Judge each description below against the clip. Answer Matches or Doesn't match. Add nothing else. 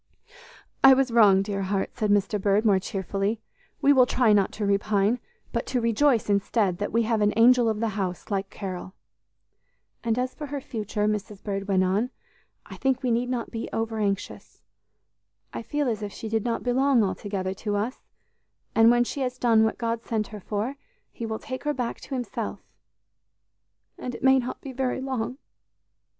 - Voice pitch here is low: Doesn't match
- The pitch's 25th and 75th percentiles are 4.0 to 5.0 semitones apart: Doesn't match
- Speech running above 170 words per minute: Matches